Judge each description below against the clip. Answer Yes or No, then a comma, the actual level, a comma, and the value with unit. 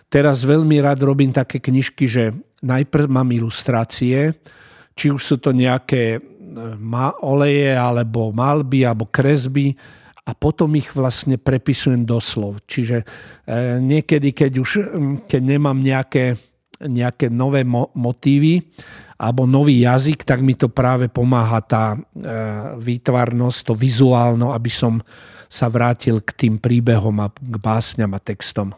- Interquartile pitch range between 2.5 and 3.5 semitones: Yes, average, 2.9 semitones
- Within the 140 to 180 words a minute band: No, average, 125 wpm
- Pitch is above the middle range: No, low, 130 Hz